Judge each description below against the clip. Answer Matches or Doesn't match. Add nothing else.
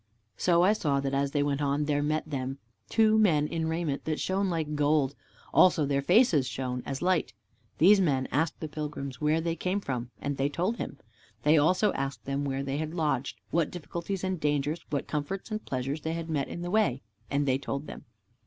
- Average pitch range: Matches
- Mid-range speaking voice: Matches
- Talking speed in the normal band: Doesn't match